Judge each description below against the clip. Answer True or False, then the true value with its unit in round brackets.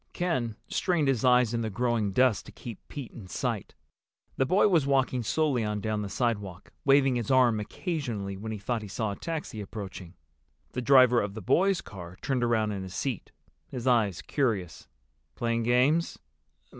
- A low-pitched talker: True (120 Hz)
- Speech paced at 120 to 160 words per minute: False (180 wpm)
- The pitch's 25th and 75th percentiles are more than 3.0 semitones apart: True (4.2 semitones)